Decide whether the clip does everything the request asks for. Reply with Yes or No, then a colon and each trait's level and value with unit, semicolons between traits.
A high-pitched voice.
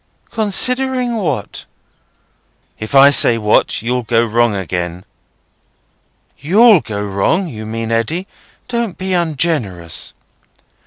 No: low, 125 Hz